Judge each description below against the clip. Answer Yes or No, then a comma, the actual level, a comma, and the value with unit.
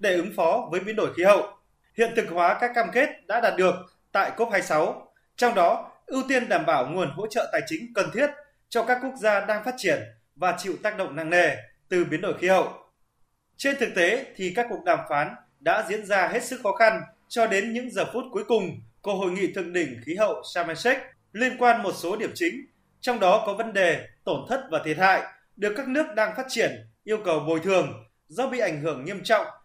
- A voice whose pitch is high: Yes, high, 210 Hz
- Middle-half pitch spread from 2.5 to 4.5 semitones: No, wide, 5.6 semitones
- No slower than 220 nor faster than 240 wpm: Yes, average, 230 wpm